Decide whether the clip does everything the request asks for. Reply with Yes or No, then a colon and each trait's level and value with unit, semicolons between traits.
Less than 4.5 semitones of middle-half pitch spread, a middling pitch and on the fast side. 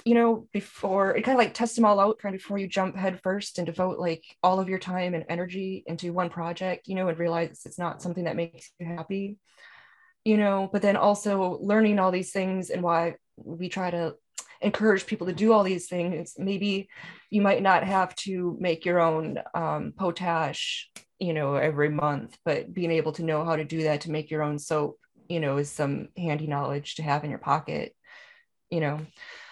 Yes: average, 3.3 semitones; medium, 180 Hz; fast, 210 wpm